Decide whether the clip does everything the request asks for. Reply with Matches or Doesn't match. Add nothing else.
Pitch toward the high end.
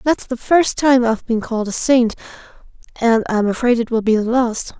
Matches